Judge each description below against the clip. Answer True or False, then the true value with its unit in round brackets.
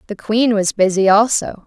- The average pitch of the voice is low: False (210 Hz)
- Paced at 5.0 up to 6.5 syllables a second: False (4.7 syllables/s)